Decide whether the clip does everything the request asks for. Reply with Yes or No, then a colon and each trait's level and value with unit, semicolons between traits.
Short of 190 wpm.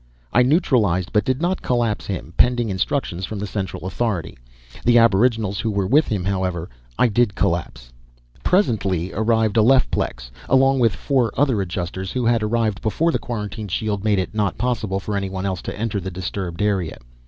Yes: average, 175 wpm